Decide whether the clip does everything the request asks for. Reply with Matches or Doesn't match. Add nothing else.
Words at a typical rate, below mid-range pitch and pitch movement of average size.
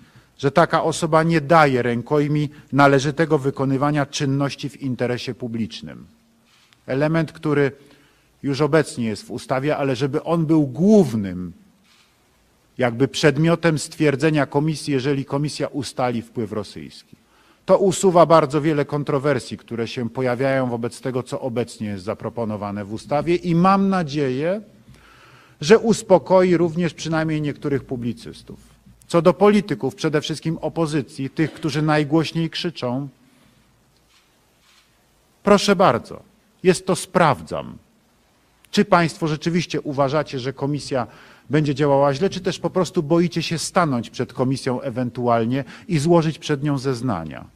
Doesn't match